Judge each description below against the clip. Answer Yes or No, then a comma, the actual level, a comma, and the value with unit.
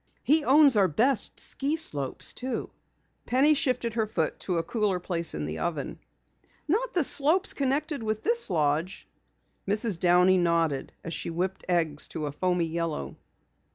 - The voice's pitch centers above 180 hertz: Yes, high, 190 Hz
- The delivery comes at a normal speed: Yes, average, 155 wpm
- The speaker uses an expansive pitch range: Yes, wide, 8.3 semitones